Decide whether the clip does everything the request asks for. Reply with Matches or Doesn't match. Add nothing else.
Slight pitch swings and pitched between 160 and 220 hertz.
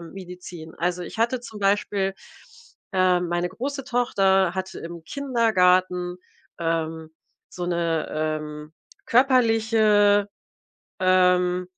Doesn't match